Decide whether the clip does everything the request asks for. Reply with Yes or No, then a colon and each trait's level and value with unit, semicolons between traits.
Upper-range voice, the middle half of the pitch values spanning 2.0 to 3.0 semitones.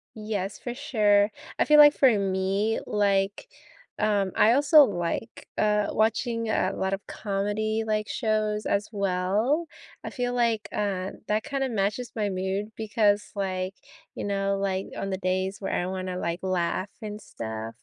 Yes: high, 205 Hz; narrow, 2.4 semitones